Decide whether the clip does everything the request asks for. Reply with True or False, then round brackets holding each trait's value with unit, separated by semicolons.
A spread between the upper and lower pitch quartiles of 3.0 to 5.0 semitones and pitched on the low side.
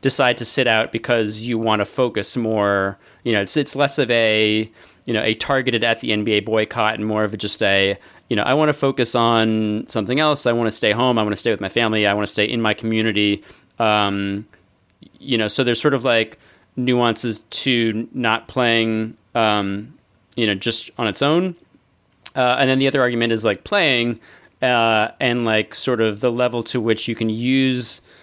False (2.4 semitones; 115 Hz)